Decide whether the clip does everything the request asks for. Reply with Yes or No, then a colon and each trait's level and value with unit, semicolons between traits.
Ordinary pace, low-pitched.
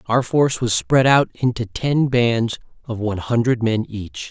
Yes: average, 195 wpm; low, 120 Hz